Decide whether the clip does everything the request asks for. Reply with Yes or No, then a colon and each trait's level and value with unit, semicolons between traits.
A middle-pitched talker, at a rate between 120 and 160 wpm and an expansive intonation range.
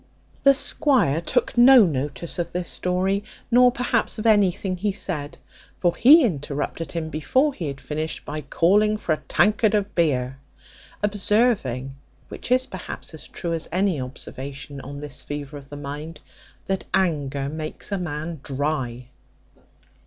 Yes: medium, 165 Hz; average, 150 wpm; wide, 6.2 semitones